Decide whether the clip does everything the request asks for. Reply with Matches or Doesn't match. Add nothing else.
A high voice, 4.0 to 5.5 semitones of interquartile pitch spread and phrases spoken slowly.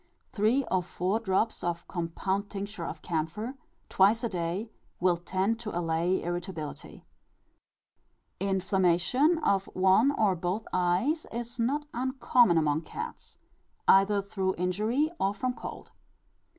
Matches